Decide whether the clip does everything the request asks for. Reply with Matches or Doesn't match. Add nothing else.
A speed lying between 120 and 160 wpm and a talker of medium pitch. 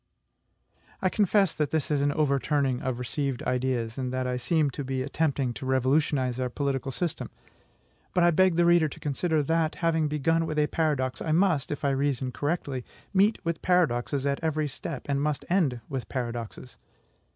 Doesn't match